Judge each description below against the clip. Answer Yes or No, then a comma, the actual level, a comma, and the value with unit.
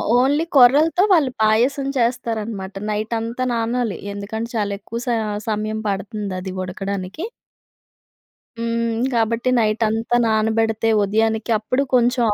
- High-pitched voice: Yes, high, 225 Hz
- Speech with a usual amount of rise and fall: No, narrow, 2.1 semitones